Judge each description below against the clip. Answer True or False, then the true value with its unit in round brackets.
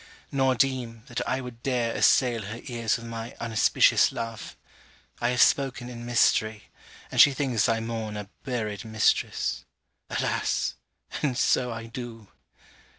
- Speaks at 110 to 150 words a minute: True (145 wpm)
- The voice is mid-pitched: False (115 Hz)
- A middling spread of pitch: False (1.9 semitones)